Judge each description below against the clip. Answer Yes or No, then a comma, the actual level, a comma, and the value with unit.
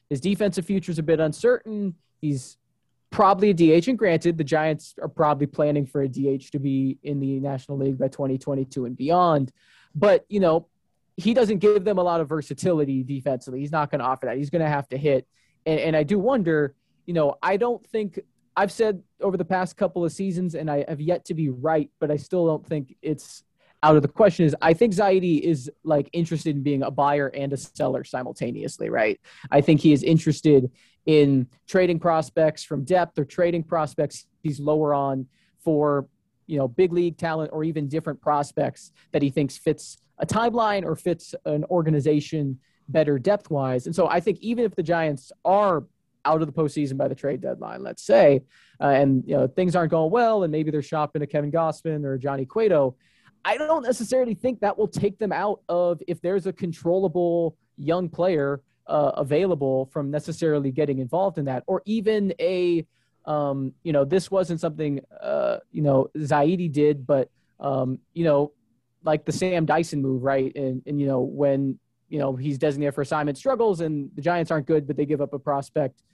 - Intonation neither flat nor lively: Yes, average, 3.9 semitones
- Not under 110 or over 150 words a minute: No, average, 200 wpm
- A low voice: No, medium, 155 Hz